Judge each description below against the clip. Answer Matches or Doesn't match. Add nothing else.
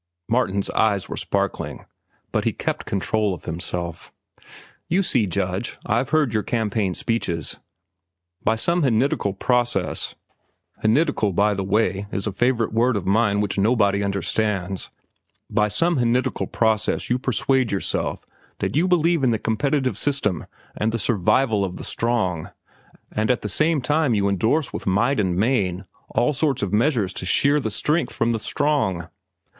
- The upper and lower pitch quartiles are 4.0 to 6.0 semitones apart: Matches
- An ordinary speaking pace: Matches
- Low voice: Matches